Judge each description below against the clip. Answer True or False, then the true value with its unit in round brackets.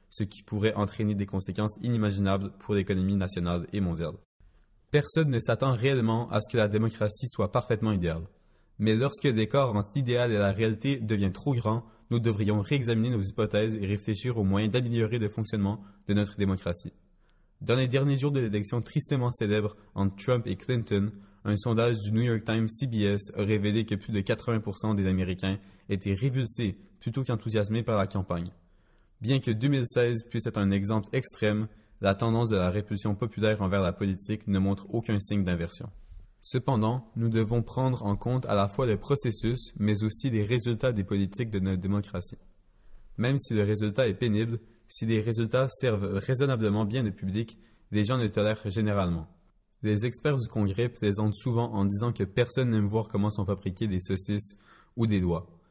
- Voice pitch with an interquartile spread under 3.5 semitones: True (2.9 semitones)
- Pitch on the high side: False (105 Hz)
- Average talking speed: True (180 wpm)